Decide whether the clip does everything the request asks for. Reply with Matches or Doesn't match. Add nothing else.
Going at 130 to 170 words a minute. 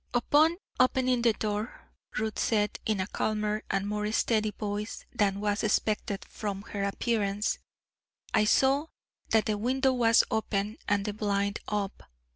Matches